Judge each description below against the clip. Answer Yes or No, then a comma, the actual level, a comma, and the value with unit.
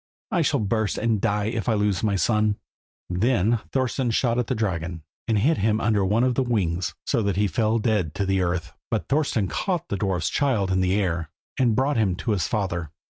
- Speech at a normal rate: No, fast, 215 wpm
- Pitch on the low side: Yes, low, 105 Hz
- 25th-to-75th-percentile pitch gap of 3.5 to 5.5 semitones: Yes, average, 3.8 semitones